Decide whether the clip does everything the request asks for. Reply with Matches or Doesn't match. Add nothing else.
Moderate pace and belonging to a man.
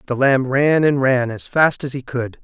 Doesn't match